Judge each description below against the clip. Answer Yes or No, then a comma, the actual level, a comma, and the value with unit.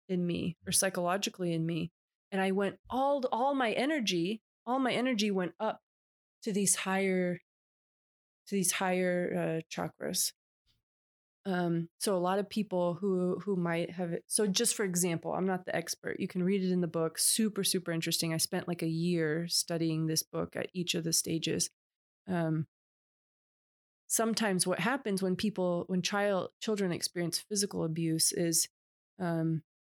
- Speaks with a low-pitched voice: No, medium, 180 Hz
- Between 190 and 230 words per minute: No, average, 165 wpm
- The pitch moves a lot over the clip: No, average, 3.1 semitones